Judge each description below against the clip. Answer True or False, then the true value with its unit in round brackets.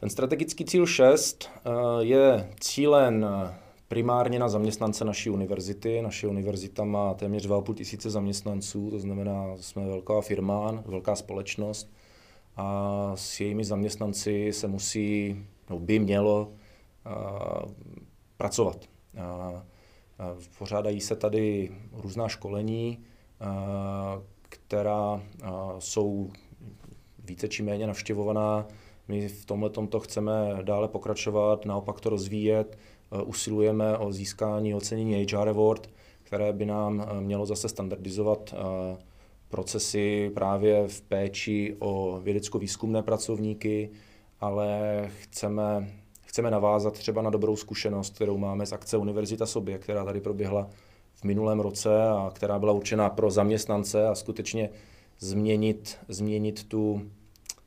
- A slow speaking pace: True (110 wpm)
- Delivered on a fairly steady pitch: True (1.2 semitones)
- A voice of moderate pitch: False (105 Hz)